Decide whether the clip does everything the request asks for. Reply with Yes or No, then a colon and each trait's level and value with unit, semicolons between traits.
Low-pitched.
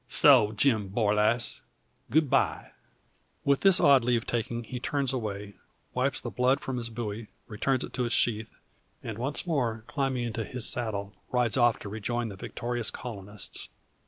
Yes: low, 120 Hz